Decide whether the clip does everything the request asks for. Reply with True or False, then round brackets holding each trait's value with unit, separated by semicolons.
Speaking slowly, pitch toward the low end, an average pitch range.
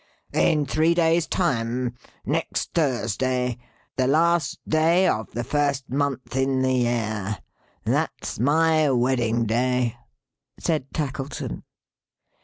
True (105 wpm; 130 Hz; 4.4 semitones)